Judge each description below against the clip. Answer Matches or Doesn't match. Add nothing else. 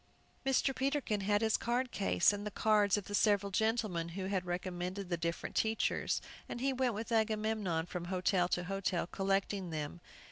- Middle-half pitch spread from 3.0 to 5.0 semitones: Matches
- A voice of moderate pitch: Doesn't match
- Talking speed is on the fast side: Doesn't match